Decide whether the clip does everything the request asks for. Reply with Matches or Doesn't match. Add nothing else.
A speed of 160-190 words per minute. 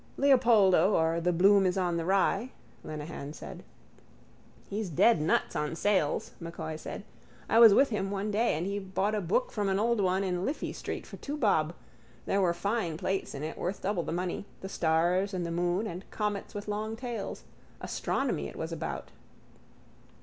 Matches